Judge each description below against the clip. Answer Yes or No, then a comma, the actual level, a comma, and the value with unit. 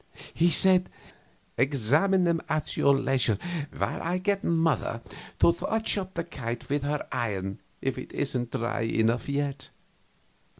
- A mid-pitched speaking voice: Yes, medium, 145 Hz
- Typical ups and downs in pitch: No, wide, 6.3 semitones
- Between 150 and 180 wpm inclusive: No, average, 140 wpm